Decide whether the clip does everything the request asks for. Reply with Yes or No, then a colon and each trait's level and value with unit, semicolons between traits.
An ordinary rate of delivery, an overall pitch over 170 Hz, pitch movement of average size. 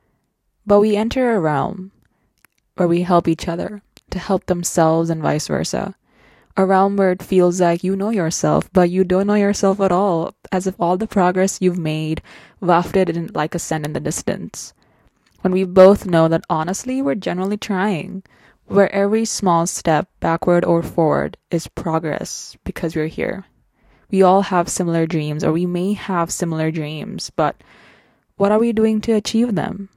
Yes: average, 175 wpm; medium, 185 Hz; average, 3.0 semitones